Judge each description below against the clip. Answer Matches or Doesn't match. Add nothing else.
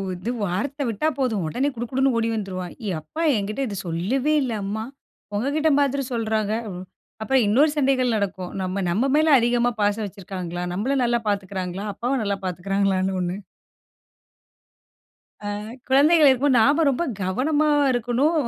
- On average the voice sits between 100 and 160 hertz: Doesn't match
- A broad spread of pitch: Matches